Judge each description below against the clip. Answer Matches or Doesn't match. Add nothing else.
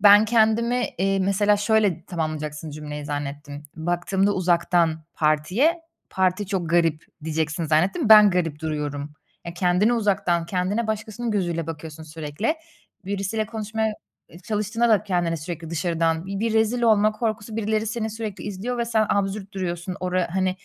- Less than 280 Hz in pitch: Matches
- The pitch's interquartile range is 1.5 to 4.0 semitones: Doesn't match